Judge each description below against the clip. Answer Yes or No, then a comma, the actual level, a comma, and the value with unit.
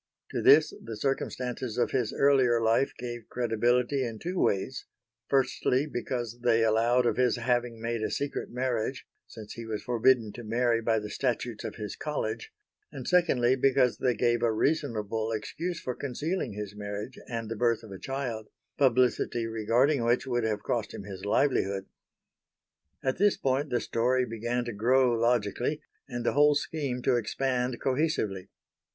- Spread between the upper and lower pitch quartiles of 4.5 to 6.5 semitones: No, narrow, 2.6 semitones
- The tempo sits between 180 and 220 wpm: No, average, 165 wpm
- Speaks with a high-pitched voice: No, low, 120 Hz